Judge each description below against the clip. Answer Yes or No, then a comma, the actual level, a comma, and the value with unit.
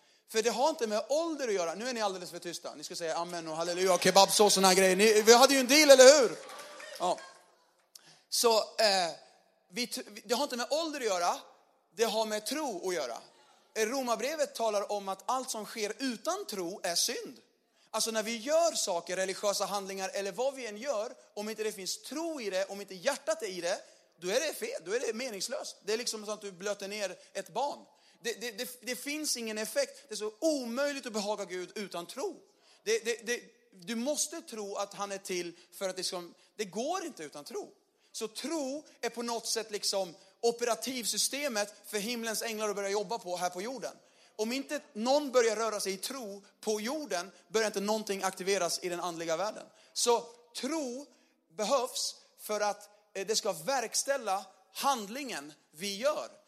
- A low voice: No, high, 220 Hz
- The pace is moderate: No, fast, 200 wpm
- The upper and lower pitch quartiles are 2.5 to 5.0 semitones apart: No, wide, 5.4 semitones